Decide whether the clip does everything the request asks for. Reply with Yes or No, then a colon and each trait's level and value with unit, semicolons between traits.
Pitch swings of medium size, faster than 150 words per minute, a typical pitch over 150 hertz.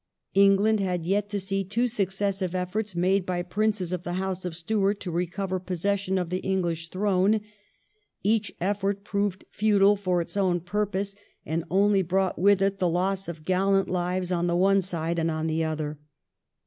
No: narrow, 2.1 semitones; average, 175 wpm; high, 190 Hz